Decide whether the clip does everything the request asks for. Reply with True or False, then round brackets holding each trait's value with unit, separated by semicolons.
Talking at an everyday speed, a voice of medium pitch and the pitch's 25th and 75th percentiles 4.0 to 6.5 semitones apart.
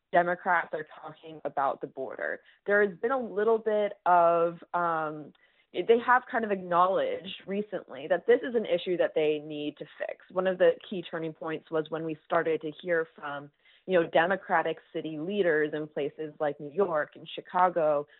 True (180 wpm; 170 Hz; 4.4 semitones)